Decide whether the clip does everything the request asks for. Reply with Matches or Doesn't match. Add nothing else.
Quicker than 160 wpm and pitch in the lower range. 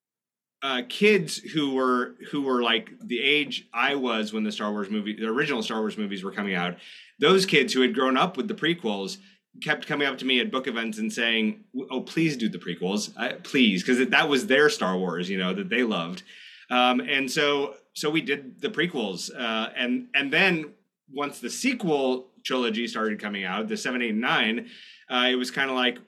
Matches